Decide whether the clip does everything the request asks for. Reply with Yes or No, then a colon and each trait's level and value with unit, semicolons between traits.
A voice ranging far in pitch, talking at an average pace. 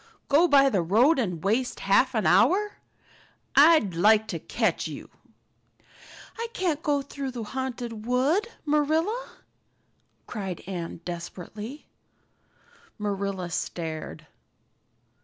No: wide, 7.0 semitones; slow, 105 wpm